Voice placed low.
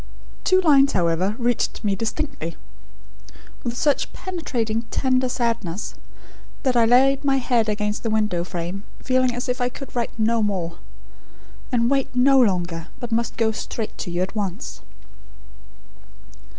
No: high, 230 Hz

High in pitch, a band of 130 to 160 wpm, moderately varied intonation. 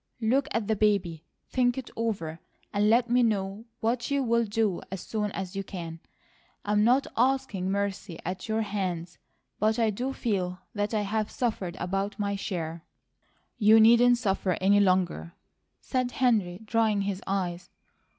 Yes: high, 205 Hz; average, 155 wpm; average, 3.3 semitones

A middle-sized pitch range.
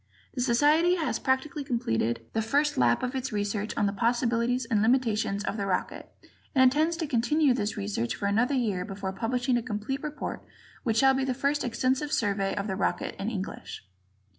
Yes: average, 4.6 semitones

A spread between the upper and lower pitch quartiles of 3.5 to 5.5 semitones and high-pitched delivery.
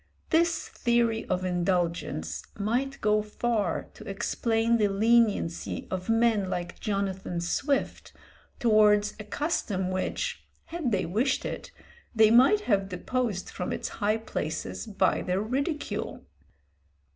Yes: average, 4.0 semitones; high, 215 Hz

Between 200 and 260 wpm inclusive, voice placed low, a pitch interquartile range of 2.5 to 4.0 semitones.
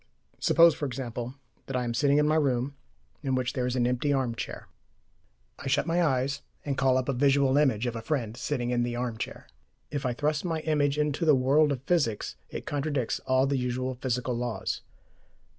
Yes: fast, 205 wpm; low, 130 Hz; average, 2.8 semitones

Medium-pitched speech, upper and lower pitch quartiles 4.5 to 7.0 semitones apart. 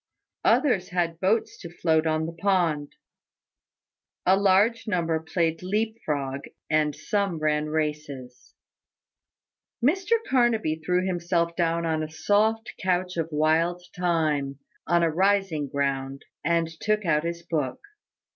No: medium, 170 Hz; average, 3.4 semitones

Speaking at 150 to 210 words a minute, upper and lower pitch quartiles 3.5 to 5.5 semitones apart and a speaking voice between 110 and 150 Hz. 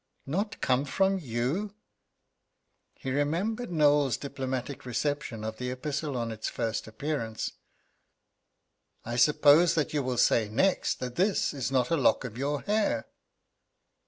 No: slow, 135 wpm; average, 4.4 semitones; medium, 140 Hz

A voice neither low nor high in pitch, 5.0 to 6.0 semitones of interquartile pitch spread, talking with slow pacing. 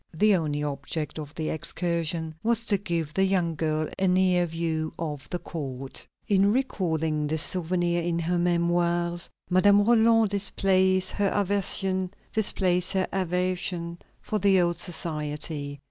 No: medium, 175 Hz; average, 3.0 semitones; slow, 130 wpm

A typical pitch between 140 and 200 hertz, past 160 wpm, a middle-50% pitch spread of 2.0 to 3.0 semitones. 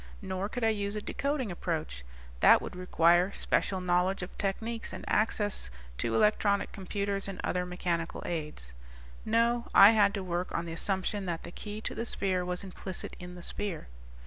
Yes: high, 190 Hz; average, 175 wpm; average, 2.7 semitones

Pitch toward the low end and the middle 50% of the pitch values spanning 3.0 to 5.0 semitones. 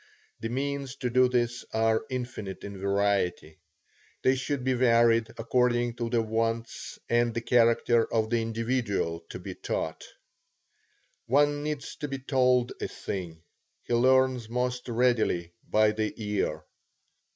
No: low, 120 Hz; narrow, 2.5 semitones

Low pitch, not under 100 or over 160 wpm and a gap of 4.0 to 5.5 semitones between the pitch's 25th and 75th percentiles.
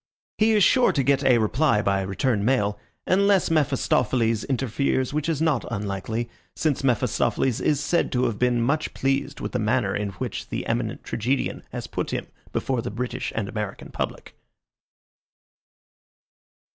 Yes: low, 125 Hz; average, 155 wpm; average, 4.7 semitones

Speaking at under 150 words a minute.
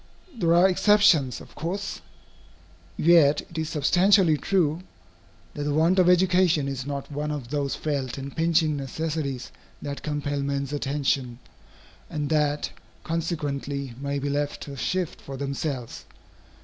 Yes: slow, 135 wpm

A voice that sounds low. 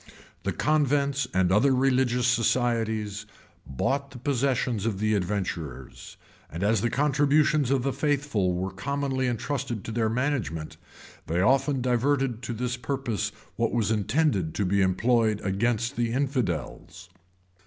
Yes: low, 120 Hz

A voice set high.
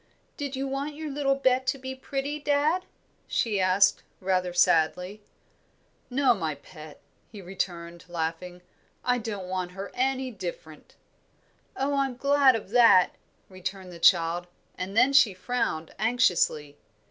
Yes: high, 215 Hz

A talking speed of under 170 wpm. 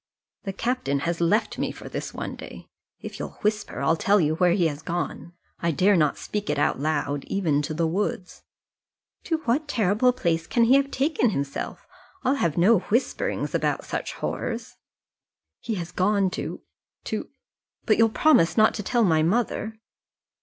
No: average, 175 wpm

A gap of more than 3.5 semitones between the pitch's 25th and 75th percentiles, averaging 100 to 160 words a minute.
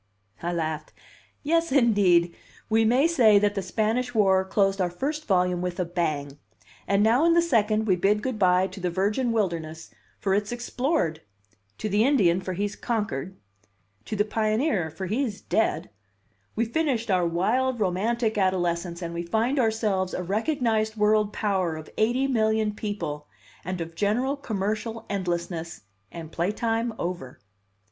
Yes: average, 4.2 semitones; average, 155 wpm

